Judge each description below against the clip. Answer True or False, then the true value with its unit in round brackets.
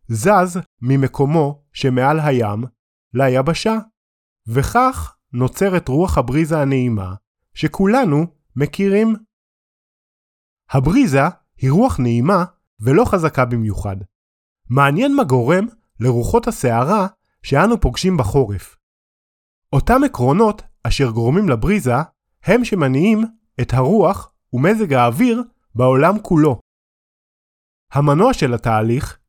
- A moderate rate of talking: False (90 wpm)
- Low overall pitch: False (145 Hz)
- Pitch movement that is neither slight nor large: False (8.4 semitones)